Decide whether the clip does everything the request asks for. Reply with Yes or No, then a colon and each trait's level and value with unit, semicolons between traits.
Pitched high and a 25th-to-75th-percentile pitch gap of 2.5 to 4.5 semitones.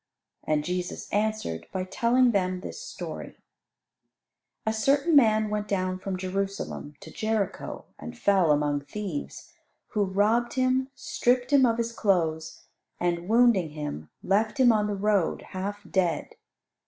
Yes: high, 200 Hz; average, 4.1 semitones